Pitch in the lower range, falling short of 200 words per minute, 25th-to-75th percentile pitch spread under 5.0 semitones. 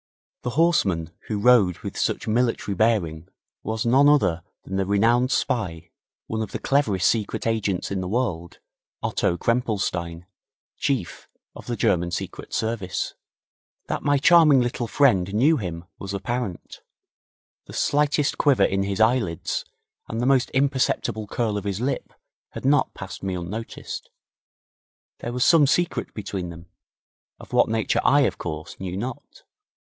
No: low, 110 Hz; average, 150 wpm; average, 5.3 semitones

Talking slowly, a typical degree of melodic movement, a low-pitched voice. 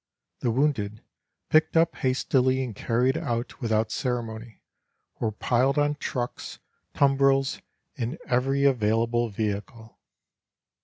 Yes: slow, 105 wpm; average, 3.2 semitones; low, 125 Hz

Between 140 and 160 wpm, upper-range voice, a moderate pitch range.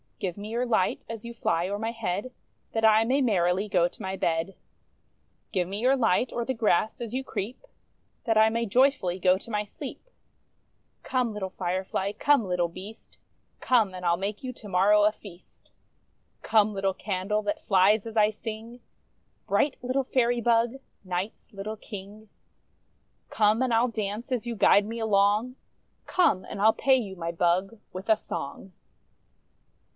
No: average, 175 wpm; high, 210 Hz; average, 3.4 semitones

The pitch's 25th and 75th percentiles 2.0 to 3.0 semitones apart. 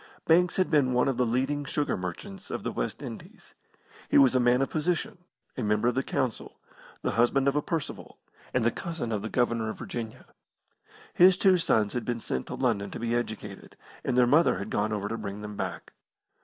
No: average, 4.6 semitones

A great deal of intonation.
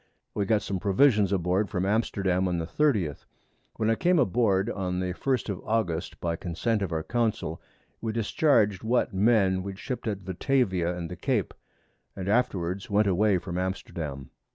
No: average, 3.7 semitones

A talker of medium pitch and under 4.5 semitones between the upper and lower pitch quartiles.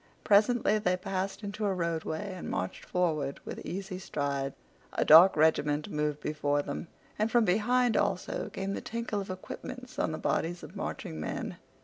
No: medium, 180 Hz; average, 5.3 semitones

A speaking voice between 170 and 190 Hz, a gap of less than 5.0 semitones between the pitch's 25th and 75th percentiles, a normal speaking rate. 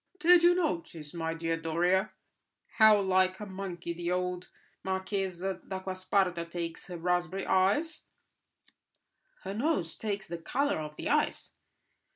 No: medium, 185 Hz; narrow, 2.5 semitones; slow, 130 wpm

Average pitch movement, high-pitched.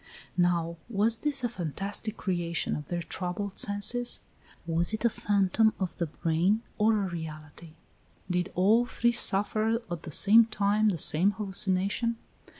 Yes: average, 4.0 semitones; high, 195 Hz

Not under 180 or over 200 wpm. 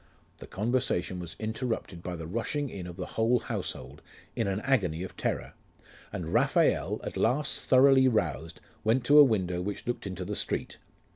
No: average, 170 wpm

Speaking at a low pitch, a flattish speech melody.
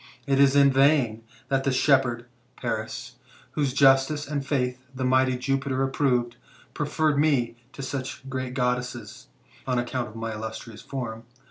Yes: low, 130 Hz; narrow, 2.2 semitones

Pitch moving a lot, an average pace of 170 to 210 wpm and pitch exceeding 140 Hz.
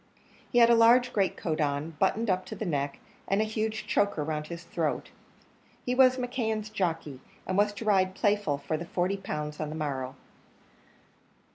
Yes: wide, 5.9 semitones; average, 180 wpm; high, 190 Hz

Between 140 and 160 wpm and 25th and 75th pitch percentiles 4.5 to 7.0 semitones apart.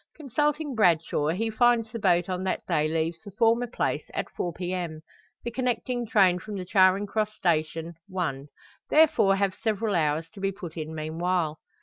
No: average, 175 wpm; average, 5.2 semitones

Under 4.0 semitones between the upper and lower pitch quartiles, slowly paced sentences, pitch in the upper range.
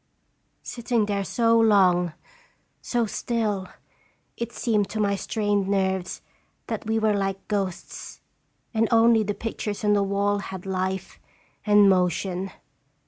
Yes: narrow, 2.5 semitones; slow, 130 wpm; high, 205 Hz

